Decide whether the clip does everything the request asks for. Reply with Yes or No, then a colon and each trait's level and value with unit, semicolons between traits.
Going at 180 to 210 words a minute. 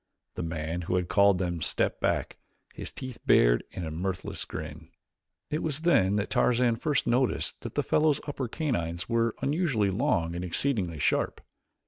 No: average, 165 wpm